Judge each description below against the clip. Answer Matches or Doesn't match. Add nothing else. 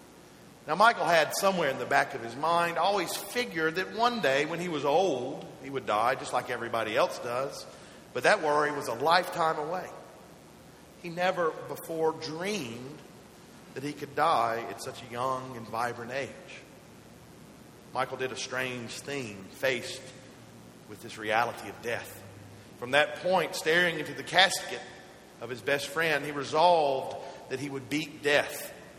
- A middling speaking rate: Matches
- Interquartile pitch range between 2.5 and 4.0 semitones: Doesn't match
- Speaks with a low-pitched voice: Doesn't match